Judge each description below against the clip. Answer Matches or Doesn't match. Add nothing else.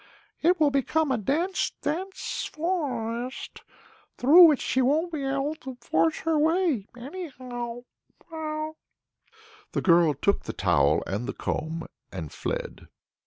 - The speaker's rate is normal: Doesn't match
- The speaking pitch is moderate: Doesn't match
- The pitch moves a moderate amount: Doesn't match